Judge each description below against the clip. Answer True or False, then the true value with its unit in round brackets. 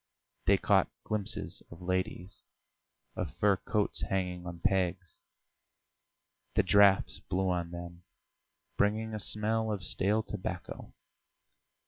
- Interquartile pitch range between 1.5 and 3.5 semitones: True (2.8 semitones)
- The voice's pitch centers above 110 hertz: False (95 Hz)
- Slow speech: True (110 wpm)